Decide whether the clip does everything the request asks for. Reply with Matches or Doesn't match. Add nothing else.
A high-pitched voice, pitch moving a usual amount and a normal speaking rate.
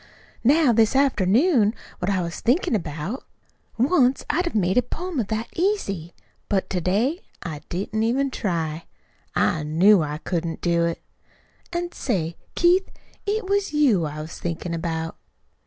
Doesn't match